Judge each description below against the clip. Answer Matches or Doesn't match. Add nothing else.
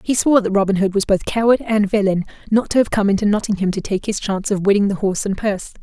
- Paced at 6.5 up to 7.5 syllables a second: Matches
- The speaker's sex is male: Doesn't match